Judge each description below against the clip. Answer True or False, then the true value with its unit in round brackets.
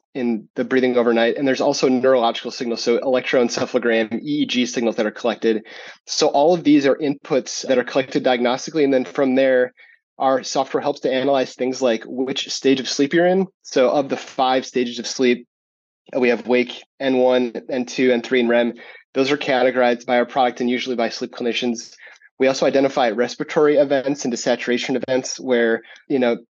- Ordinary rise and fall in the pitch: False (1.8 semitones)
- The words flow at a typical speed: True (185 wpm)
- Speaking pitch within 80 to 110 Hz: False (125 Hz)